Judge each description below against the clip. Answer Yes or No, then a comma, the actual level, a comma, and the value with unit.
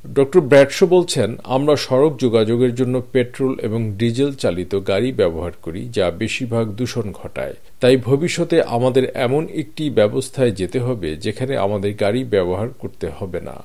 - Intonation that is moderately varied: Yes, average, 3.5 semitones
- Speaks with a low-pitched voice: Yes, low, 125 Hz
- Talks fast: Yes, fast, 145 wpm